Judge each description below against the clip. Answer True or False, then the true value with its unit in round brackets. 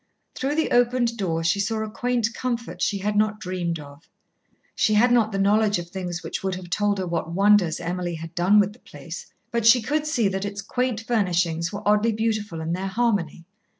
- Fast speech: True (210 wpm)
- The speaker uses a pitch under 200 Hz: False (205 Hz)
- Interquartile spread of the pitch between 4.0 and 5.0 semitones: True (4.3 semitones)